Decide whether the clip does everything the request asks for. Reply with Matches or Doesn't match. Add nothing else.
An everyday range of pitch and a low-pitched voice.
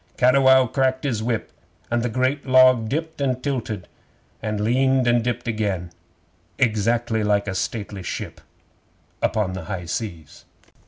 Matches